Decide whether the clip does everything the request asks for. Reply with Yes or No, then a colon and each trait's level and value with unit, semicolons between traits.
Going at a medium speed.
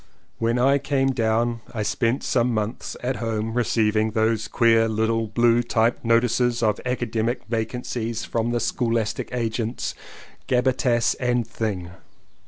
No: slow, 130 wpm